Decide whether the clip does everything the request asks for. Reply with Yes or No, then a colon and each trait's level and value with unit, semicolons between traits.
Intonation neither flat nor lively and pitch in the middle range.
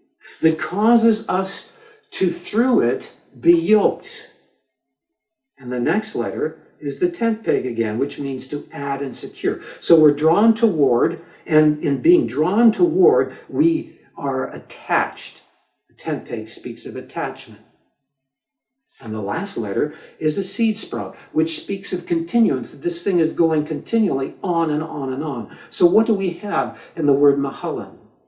No: wide, 8.0 semitones; medium, 170 Hz